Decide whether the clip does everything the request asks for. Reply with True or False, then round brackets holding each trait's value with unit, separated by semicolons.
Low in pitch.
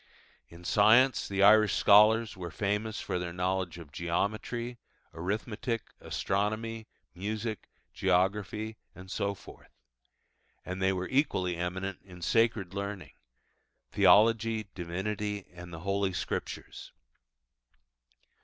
True (100 Hz)